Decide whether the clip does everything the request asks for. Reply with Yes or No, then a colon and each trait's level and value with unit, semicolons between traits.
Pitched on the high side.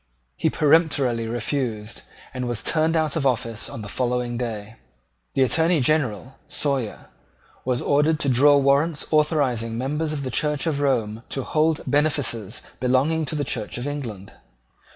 No: low, 135 Hz